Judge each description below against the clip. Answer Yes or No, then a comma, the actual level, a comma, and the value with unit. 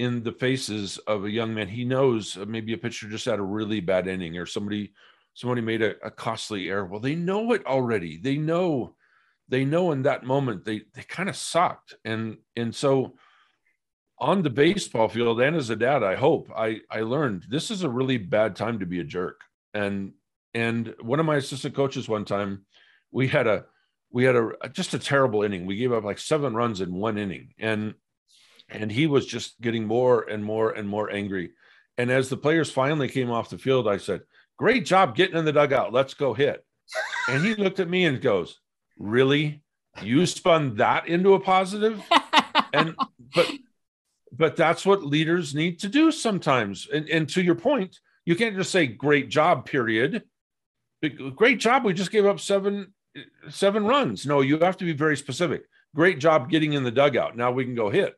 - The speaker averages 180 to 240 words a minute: Yes, average, 200 wpm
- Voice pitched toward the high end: No, low, 135 Hz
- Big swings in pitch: Yes, wide, 6.9 semitones